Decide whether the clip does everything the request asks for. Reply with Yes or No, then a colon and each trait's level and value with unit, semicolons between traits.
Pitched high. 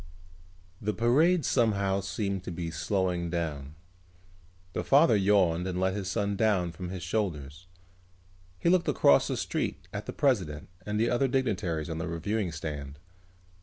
No: very low, 95 Hz